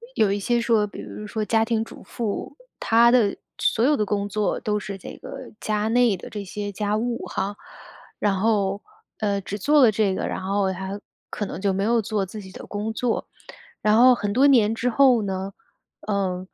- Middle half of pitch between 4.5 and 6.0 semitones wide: No, narrow, 2.4 semitones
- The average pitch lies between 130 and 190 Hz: No, high, 210 Hz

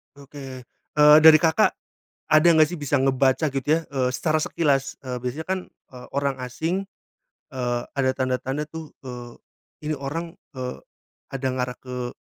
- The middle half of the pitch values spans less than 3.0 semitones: No, average, 3.4 semitones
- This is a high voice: No, low, 135 Hz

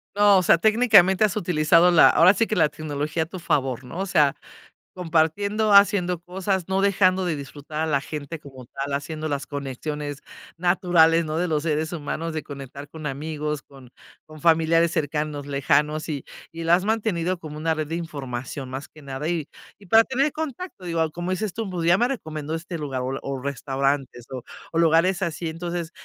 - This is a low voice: No, medium, 160 Hz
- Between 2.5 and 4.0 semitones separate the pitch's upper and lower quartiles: Yes, average, 3.7 semitones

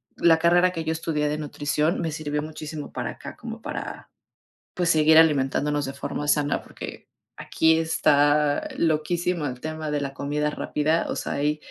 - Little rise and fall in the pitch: Yes, narrow, 1.6 semitones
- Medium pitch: Yes, medium, 150 Hz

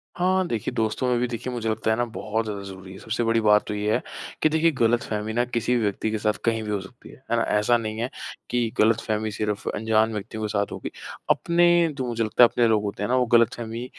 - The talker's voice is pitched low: Yes, low, 110 Hz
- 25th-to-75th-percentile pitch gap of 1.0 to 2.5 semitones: Yes, narrow, 2.1 semitones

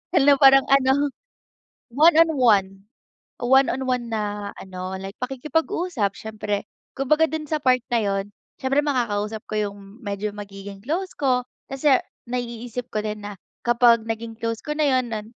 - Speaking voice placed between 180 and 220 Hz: No, high, 240 Hz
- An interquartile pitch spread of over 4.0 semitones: Yes, average, 4.6 semitones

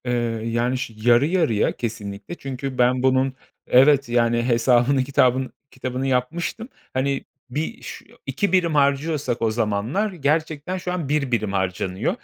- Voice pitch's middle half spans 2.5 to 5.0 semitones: Yes, average, 4.0 semitones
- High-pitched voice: No, low, 130 Hz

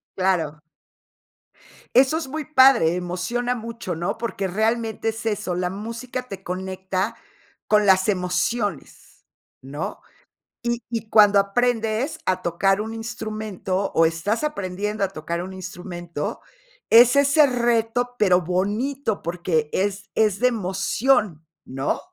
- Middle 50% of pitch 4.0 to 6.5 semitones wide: Yes, average, 4.3 semitones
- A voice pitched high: Yes, high, 205 Hz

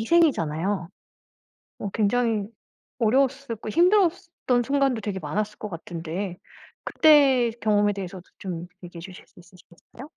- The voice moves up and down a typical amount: No, wide, 6.8 semitones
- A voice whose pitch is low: No, high, 210 Hz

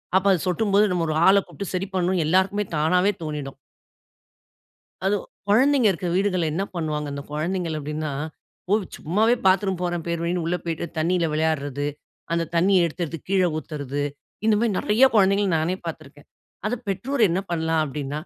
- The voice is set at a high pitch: No, medium, 175 Hz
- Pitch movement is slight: No, average, 3.8 semitones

